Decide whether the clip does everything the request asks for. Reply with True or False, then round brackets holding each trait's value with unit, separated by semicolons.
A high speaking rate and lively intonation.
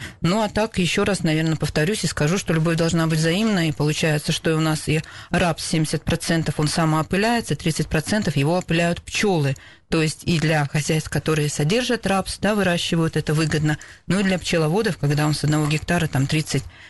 False (180 wpm; 2.6 semitones)